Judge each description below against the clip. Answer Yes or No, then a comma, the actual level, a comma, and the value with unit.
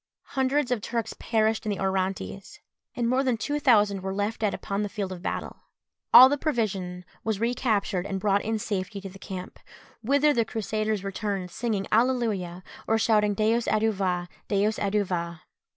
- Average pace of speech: Yes, average, 170 wpm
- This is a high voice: Yes, high, 210 Hz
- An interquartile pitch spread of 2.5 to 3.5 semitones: Yes, average, 3.0 semitones